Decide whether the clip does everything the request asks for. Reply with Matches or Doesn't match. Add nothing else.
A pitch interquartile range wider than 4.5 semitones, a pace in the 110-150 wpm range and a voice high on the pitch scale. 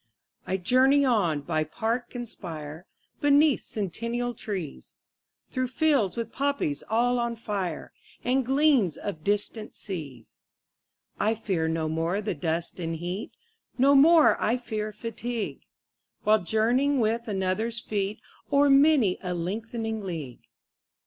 Matches